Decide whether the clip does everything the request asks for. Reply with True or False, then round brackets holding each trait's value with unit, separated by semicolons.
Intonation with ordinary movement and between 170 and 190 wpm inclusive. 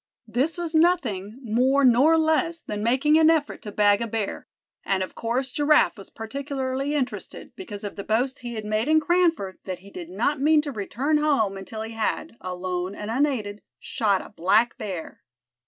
False (6.3 semitones; 185 wpm)